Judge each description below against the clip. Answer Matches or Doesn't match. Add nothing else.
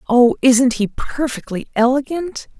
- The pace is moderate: Doesn't match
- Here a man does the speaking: Doesn't match